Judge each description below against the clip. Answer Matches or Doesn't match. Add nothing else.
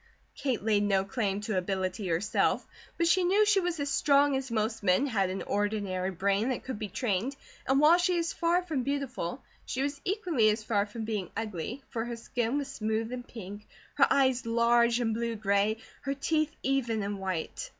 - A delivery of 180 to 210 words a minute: Matches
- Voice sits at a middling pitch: Doesn't match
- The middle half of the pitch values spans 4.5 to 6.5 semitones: Matches